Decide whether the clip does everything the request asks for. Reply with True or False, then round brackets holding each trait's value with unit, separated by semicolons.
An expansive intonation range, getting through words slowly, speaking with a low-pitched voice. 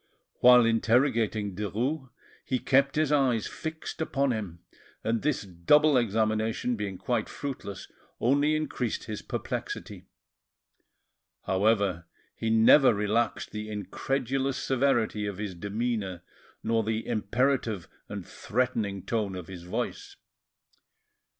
False (4.3 semitones; 110 wpm; 115 Hz)